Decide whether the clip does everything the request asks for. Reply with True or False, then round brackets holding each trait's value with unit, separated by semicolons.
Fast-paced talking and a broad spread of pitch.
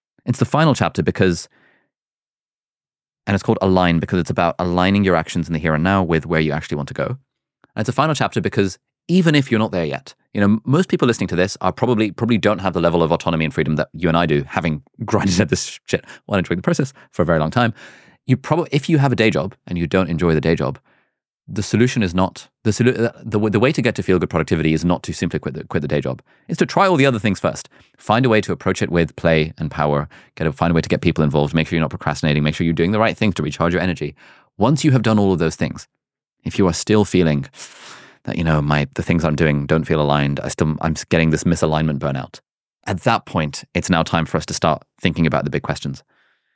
True (265 wpm; 5.7 semitones)